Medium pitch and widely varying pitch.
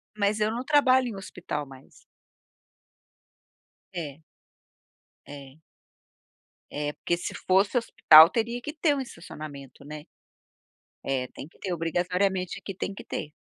Yes: medium, 180 Hz; wide, 6.5 semitones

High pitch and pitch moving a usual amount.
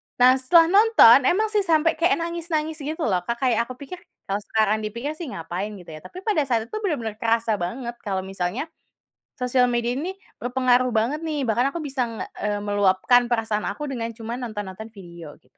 No: high, 245 Hz; wide, 6.0 semitones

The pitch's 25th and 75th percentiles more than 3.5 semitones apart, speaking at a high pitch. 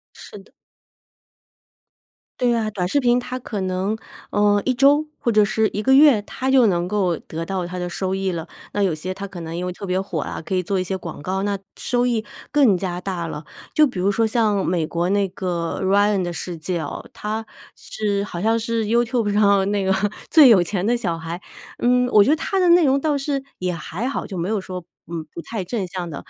Yes: average, 4.3 semitones; high, 200 Hz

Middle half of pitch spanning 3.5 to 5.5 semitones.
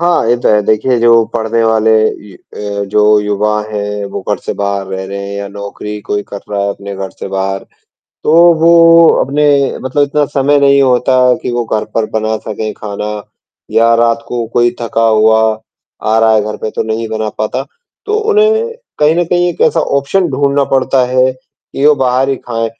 Yes: average, 4.5 semitones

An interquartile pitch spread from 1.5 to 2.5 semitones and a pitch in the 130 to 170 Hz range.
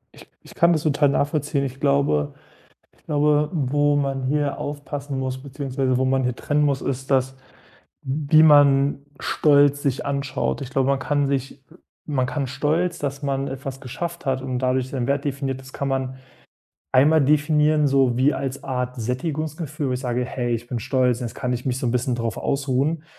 Yes: narrow, 1.9 semitones; low, 135 Hz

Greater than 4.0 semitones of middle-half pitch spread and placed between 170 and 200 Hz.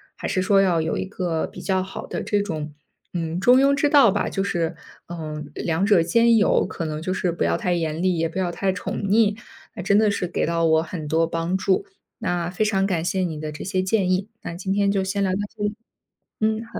No: average, 3.3 semitones; medium, 185 Hz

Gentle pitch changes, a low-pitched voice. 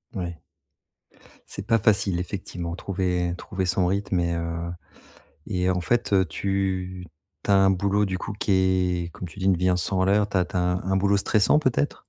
Yes: narrow, 1.9 semitones; very low, 95 Hz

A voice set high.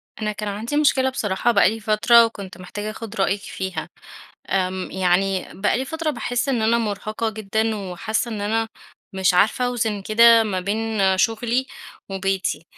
Yes: high, 215 Hz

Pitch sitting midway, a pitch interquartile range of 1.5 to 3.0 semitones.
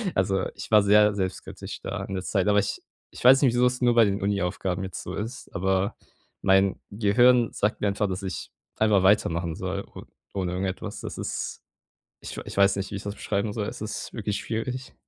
No: low, 100 Hz; narrow, 2.4 semitones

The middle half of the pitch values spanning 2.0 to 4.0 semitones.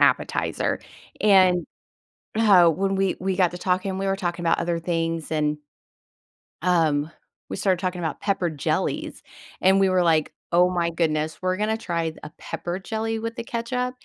Yes: average, 2.7 semitones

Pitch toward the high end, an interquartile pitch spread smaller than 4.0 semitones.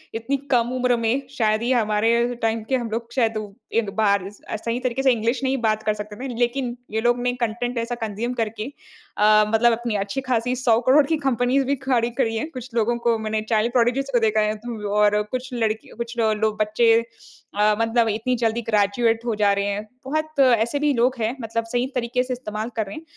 Yes: high, 230 Hz; narrow, 2.4 semitones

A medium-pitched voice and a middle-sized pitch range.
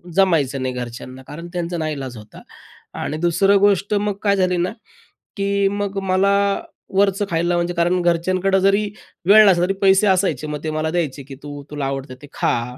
Yes: medium, 175 Hz; average, 5.0 semitones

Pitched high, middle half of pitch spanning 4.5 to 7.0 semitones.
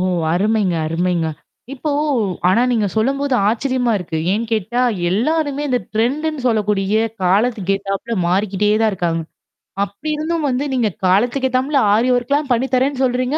Yes: high, 235 Hz; average, 5.0 semitones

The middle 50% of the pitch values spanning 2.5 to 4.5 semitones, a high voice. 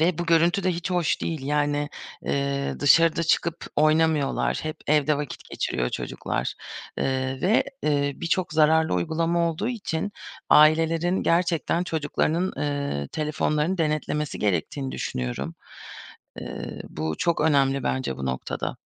No: average, 3.1 semitones; medium, 155 Hz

